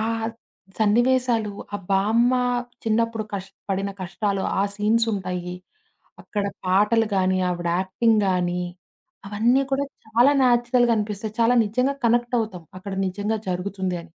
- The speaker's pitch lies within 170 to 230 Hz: Yes, high, 210 Hz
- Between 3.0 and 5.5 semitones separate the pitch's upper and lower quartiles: Yes, average, 3.5 semitones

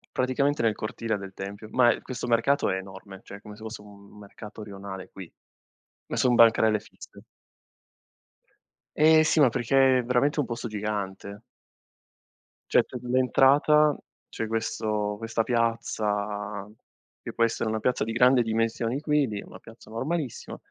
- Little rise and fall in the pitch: No, average, 3.5 semitones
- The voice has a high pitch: No, low, 115 Hz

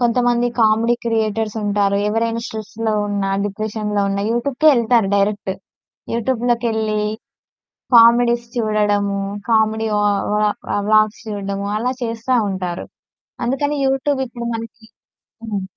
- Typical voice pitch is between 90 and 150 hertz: No, high, 220 Hz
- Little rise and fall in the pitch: Yes, narrow, 2.3 semitones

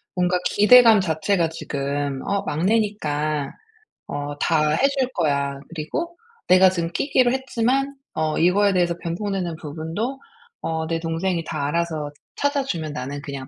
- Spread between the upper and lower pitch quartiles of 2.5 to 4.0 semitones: No, average, 5.1 semitones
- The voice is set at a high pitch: No, medium, 170 Hz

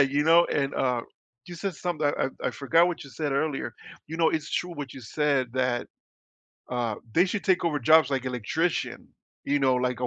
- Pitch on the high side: No, medium, 145 Hz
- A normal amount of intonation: Yes, average, 4.2 semitones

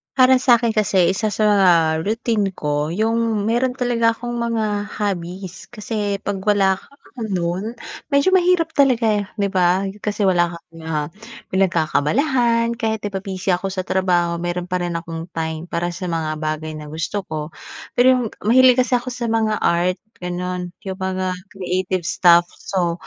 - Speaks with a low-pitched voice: No, high, 190 Hz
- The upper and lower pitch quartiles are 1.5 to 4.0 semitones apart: No, average, 4.7 semitones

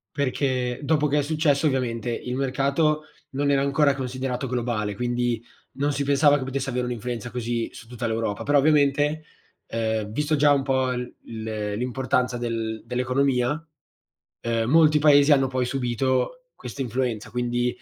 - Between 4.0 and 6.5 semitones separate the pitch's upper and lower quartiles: No, average, 2.9 semitones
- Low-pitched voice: Yes, low, 130 Hz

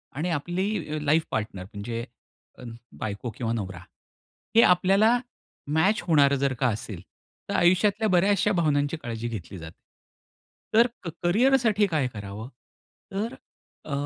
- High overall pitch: No, medium, 155 Hz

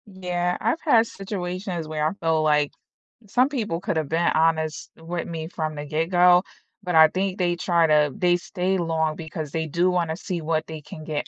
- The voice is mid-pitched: Yes, medium, 170 Hz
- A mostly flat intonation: Yes, narrow, 2.3 semitones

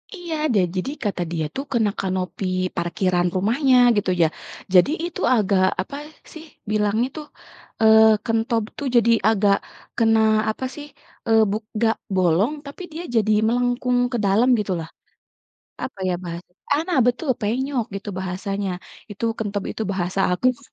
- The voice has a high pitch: Yes, high, 215 Hz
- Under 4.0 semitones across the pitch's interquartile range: No, average, 4.3 semitones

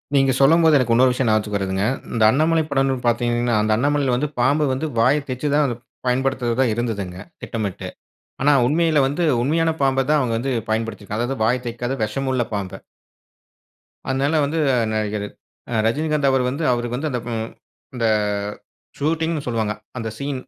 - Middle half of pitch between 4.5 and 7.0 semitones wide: No, average, 4.0 semitones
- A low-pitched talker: Yes, low, 130 Hz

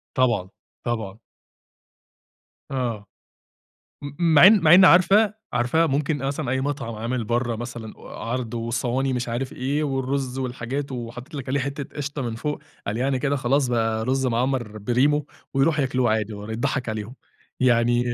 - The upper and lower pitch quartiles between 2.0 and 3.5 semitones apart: Yes, average, 3.1 semitones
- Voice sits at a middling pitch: No, low, 130 Hz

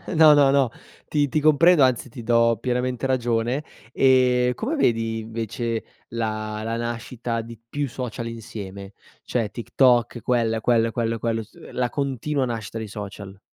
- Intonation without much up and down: Yes, narrow, 2.3 semitones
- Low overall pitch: Yes, low, 115 Hz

